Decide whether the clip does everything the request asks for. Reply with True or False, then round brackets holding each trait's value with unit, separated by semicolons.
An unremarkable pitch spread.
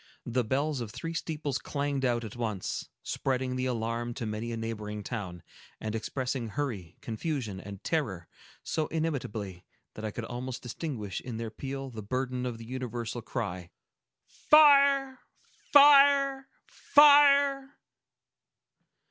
False (5.9 semitones)